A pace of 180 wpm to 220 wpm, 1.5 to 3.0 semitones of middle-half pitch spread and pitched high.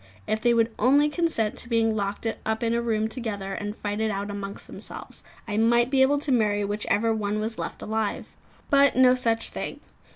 Yes: average, 200 wpm; narrow, 2.4 semitones; high, 220 Hz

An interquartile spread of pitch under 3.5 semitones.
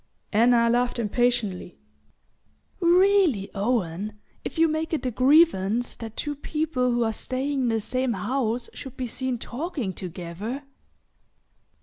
No: average, 4.5 semitones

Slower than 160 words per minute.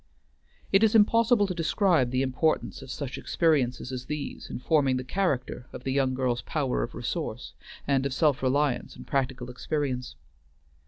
No: average, 170 wpm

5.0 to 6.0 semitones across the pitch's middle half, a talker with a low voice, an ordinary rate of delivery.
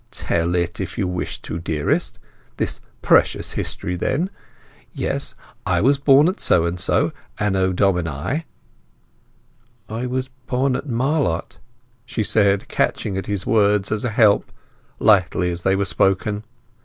Yes: wide, 5.6 semitones; low, 100 Hz; average, 145 wpm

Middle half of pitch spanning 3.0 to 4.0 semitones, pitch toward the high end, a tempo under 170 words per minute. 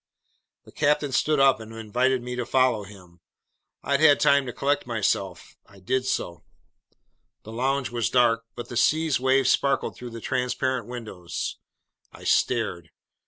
No: average, 3.3 semitones; low, 125 Hz; average, 155 wpm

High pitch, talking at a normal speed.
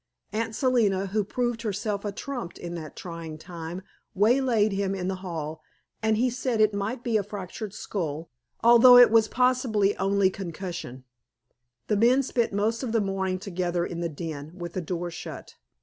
Yes: high, 200 Hz; average, 175 wpm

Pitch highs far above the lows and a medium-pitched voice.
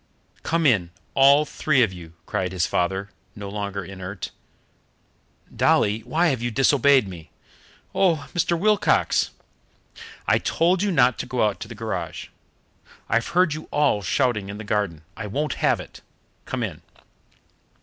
No: wide, 6.9 semitones; low, 115 Hz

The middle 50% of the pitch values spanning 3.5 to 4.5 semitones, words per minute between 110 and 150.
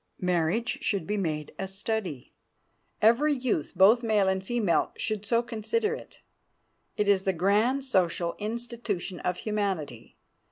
Yes: average, 4.1 semitones; slow, 135 wpm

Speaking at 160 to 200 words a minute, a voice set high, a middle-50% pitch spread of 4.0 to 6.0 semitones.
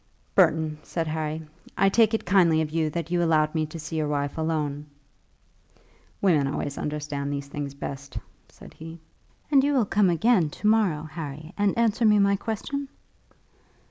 No: average, 170 wpm; medium, 160 Hz; average, 4.8 semitones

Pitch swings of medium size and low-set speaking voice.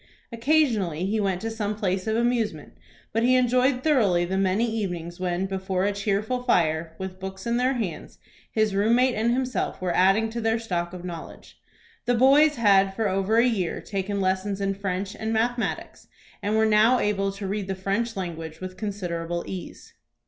No: average, 3.6 semitones; high, 200 Hz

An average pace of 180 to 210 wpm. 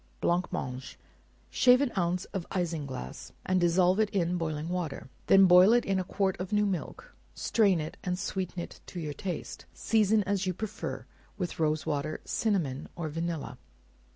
No: average, 165 wpm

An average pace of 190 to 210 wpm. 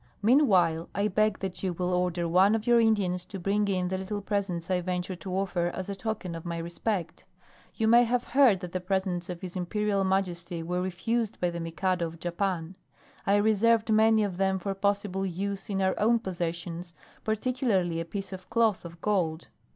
Yes: average, 195 wpm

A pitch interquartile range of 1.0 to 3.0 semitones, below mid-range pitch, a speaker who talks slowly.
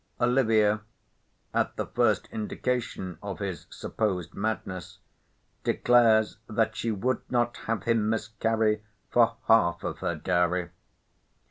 Yes: narrow, 2.6 semitones; low, 110 Hz; slow, 115 wpm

